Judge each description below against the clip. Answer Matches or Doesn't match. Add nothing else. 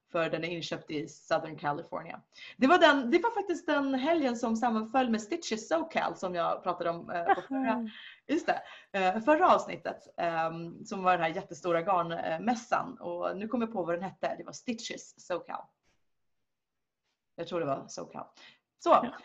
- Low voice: Doesn't match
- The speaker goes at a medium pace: Matches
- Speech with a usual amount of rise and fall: Doesn't match